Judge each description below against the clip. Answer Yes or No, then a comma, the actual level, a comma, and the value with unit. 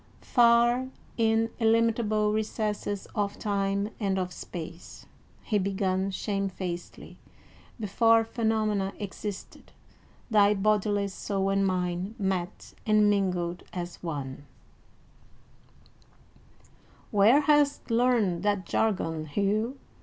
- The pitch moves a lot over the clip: No, average, 2.8 semitones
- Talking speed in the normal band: No, slow, 95 wpm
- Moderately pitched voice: No, high, 205 Hz